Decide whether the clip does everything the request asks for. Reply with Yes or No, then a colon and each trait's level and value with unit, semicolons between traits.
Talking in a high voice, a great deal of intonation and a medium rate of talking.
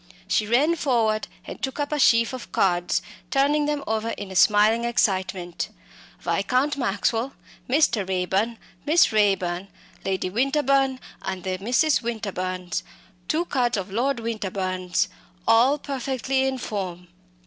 No: high, 225 Hz; wide, 5.8 semitones; slow, 130 wpm